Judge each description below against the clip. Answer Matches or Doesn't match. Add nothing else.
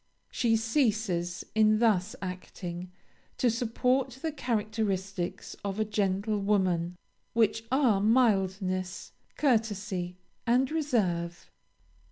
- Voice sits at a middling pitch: Doesn't match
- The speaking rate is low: Matches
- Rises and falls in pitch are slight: Doesn't match